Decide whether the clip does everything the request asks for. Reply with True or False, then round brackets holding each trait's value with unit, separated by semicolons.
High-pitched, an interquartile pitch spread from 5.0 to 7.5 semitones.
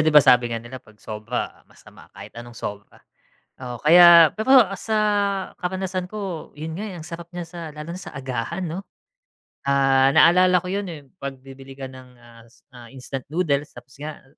False (150 Hz; 5.6 semitones)